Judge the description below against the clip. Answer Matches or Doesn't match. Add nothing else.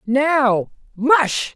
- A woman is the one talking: Matches